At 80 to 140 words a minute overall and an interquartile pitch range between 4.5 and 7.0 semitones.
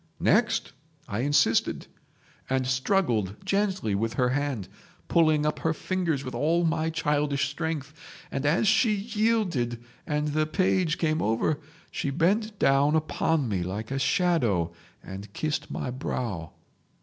Yes: slow, 135 wpm; average, 5.0 semitones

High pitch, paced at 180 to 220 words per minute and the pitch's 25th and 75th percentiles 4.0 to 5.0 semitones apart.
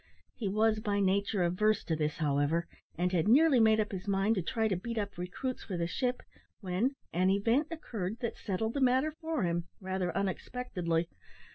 Yes: high, 200 Hz; average, 185 wpm; average, 4.5 semitones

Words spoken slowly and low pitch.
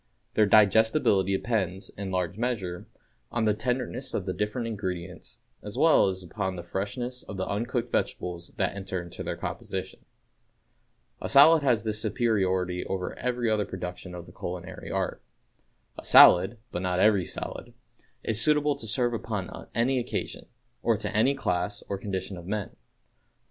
No: average, 160 wpm; low, 105 Hz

